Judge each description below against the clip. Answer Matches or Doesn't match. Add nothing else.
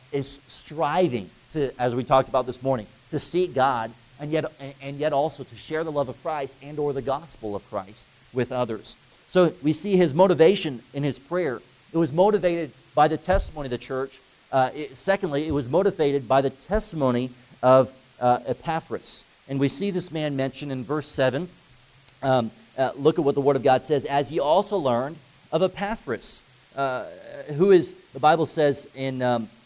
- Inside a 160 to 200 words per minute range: Matches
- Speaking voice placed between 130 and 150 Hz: Matches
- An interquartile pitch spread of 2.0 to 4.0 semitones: Matches